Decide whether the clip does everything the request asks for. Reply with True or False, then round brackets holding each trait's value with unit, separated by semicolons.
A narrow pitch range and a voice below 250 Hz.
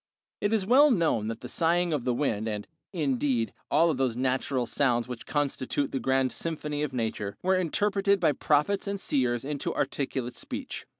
False (5.3 semitones; 140 Hz)